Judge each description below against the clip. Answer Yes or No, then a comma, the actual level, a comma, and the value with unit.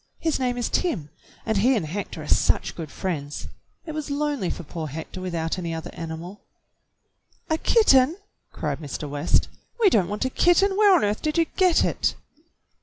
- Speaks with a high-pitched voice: Yes, high, 205 Hz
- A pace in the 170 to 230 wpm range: Yes, average, 180 wpm